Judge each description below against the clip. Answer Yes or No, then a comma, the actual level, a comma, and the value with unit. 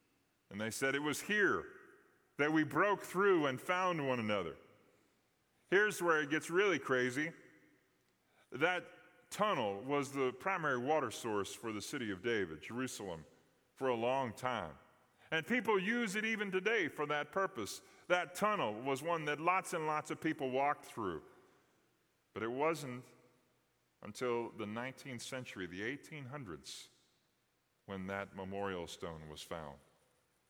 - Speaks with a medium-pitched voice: Yes, medium, 145 Hz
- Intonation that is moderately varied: No, wide, 6.9 semitones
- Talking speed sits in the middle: Yes, average, 145 wpm